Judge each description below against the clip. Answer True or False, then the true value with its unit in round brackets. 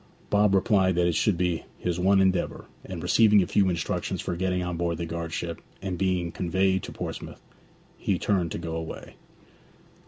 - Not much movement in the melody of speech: True (2.1 semitones)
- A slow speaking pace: False (185 wpm)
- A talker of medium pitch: False (90 Hz)